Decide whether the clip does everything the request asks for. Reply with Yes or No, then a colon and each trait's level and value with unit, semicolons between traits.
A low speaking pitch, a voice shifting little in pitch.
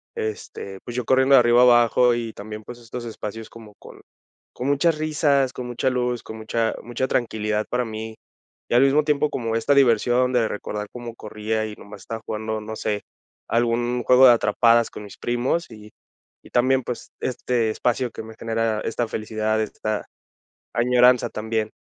Yes: low, 115 Hz; narrow, 2.2 semitones